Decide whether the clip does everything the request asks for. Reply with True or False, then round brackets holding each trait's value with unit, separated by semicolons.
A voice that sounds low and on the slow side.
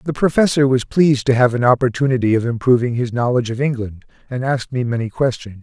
False (125 Hz; 205 wpm)